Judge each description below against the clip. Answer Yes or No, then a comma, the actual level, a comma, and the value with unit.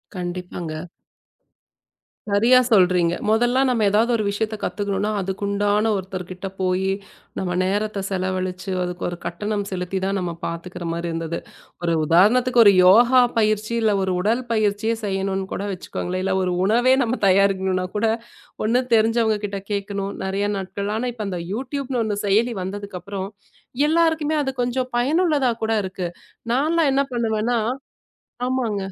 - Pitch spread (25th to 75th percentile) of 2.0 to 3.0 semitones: No, average, 3.7 semitones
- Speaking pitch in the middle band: No, high, 205 Hz